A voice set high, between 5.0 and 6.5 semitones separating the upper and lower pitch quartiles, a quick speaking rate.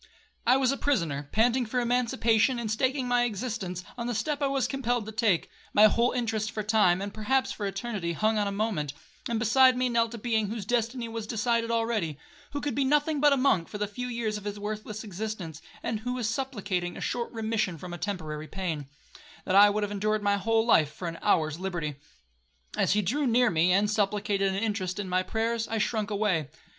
No: high, 215 Hz; average, 3.3 semitones; fast, 215 wpm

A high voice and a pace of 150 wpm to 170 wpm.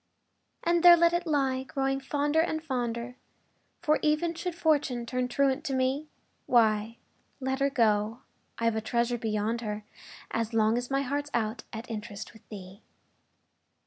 Yes: very high, 255 Hz; average, 155 wpm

